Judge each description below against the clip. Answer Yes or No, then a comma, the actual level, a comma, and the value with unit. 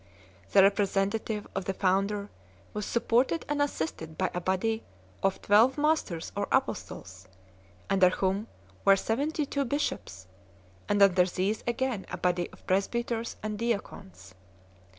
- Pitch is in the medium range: No, high, 200 Hz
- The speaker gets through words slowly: Yes, slow, 130 wpm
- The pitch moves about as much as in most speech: Yes, average, 4.0 semitones